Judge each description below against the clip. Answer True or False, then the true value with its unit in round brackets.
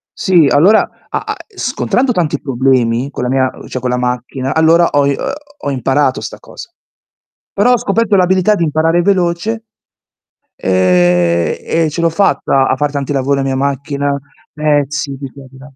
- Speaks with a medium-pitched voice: True (145 Hz)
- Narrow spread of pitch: False (4.4 semitones)